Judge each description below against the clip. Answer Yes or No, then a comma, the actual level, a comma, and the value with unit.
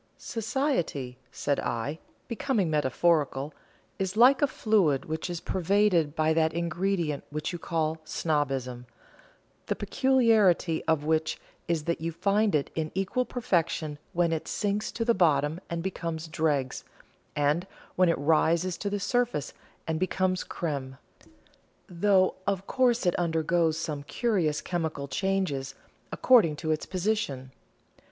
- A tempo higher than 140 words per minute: No, slow, 135 wpm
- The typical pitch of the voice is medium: Yes, medium, 165 Hz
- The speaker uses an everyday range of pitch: Yes, average, 4.2 semitones